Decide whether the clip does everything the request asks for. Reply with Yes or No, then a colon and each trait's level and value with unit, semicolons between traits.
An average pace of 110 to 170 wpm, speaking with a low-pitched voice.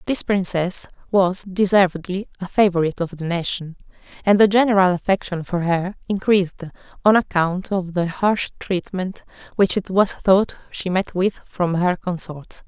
No: average, 150 wpm; medium, 185 Hz